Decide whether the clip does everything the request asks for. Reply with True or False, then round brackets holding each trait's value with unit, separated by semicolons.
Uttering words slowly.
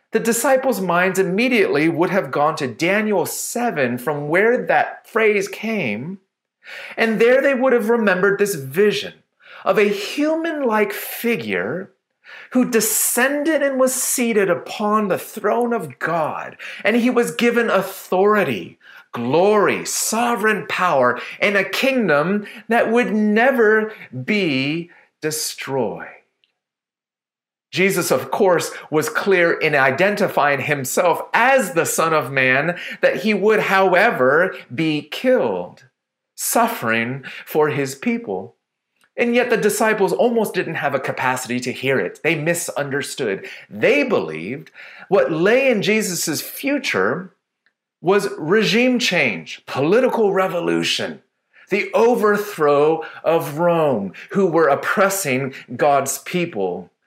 True (120 wpm)